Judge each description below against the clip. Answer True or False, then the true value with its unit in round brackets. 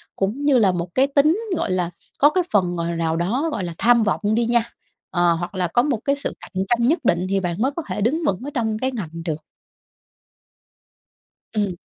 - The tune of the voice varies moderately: False (7.1 semitones)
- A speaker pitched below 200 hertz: False (215 Hz)